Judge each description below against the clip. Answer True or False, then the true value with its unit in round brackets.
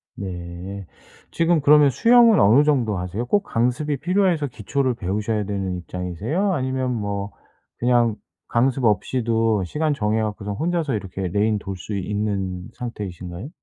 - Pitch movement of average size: False (5.9 semitones)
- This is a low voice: True (110 Hz)